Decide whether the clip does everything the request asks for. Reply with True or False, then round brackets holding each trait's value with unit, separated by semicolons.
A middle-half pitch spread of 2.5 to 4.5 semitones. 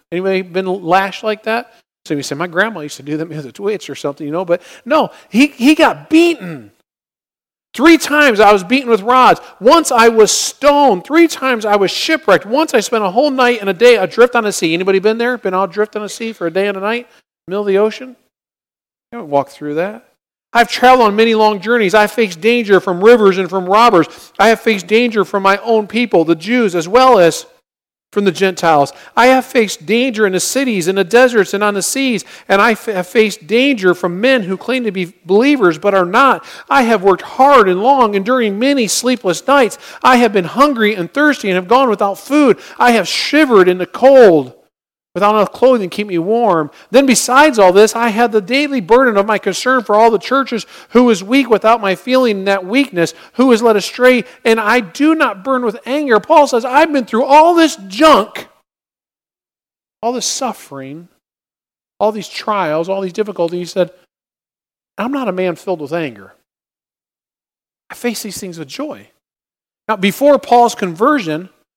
False (4.9 semitones)